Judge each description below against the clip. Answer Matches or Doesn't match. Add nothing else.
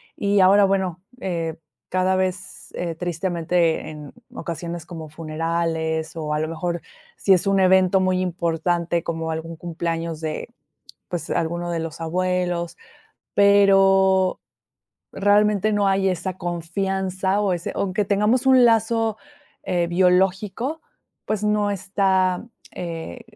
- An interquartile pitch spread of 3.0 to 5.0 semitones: Doesn't match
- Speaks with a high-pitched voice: Doesn't match